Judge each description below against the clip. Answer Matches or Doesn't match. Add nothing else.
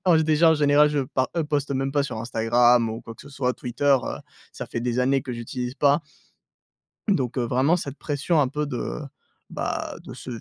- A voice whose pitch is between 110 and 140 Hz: Matches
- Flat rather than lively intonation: Doesn't match